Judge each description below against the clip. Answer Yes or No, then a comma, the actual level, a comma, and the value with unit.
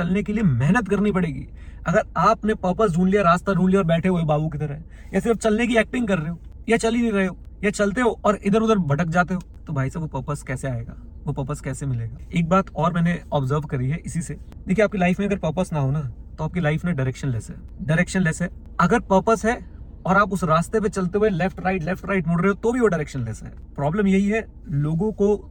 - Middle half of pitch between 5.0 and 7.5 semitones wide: Yes, wide, 5.4 semitones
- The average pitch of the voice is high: No, medium, 180 Hz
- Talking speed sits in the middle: Yes, average, 120 wpm